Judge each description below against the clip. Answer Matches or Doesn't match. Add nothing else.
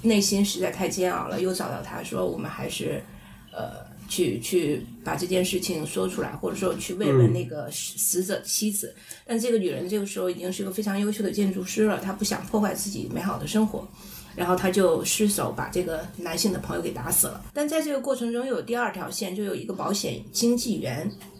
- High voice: Matches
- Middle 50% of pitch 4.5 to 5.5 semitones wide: Doesn't match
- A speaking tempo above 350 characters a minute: Doesn't match